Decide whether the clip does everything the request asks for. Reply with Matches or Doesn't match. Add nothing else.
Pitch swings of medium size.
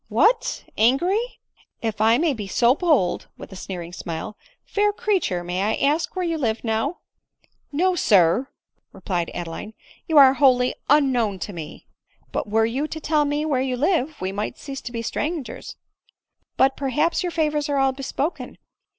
Doesn't match